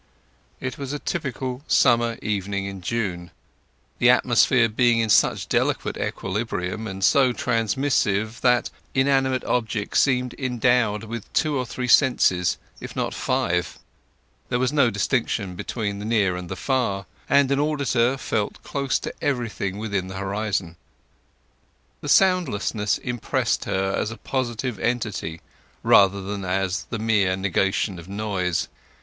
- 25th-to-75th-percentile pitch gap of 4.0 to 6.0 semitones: Yes, average, 4.5 semitones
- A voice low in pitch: Yes, low, 110 Hz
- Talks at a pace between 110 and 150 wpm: Yes, average, 140 wpm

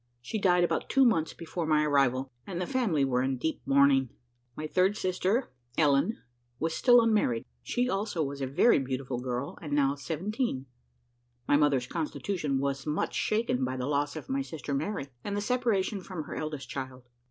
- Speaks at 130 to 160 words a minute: No, average, 180 wpm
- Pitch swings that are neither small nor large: No, wide, 6.4 semitones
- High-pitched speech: No, medium, 150 Hz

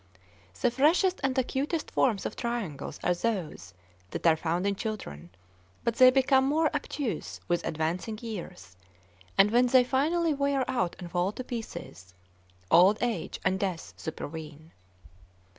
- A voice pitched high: Yes, high, 220 Hz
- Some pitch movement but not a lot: No, wide, 7.4 semitones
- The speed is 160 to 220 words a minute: No, average, 140 wpm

